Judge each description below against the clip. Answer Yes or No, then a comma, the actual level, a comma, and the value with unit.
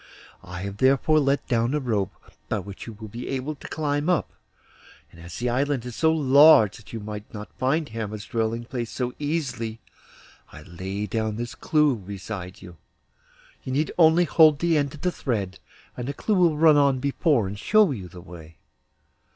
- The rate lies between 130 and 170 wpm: No, average, 190 wpm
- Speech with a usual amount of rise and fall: No, wide, 6.1 semitones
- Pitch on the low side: Yes, low, 120 Hz